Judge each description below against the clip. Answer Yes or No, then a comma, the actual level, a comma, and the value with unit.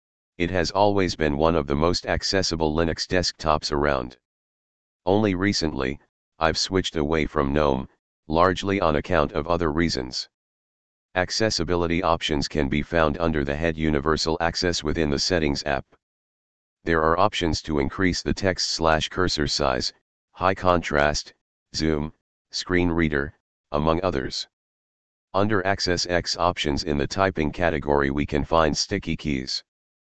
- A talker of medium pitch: No, very low, 80 Hz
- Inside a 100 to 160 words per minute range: Yes, average, 140 wpm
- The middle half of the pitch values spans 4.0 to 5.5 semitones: No, average, 3.4 semitones